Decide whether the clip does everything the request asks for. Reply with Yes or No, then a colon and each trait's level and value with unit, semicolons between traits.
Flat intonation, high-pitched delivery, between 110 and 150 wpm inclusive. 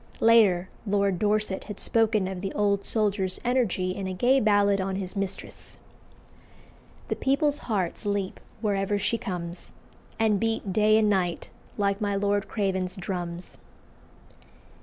Yes: narrow, 2.3 semitones; high, 200 Hz; average, 140 wpm